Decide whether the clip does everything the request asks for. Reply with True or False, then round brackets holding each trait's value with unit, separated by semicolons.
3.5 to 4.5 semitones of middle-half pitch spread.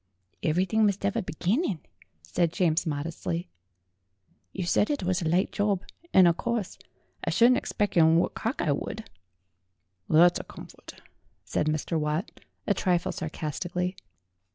True (4.1 semitones)